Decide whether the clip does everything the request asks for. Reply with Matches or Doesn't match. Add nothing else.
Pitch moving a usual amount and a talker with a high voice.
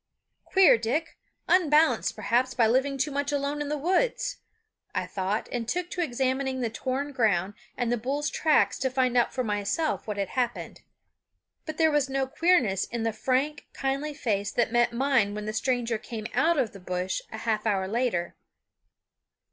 Matches